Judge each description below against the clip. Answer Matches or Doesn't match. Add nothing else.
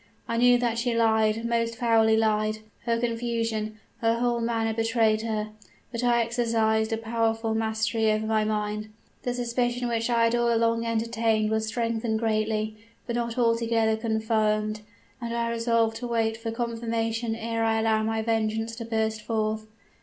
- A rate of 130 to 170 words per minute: Matches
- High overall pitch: Matches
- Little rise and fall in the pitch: Matches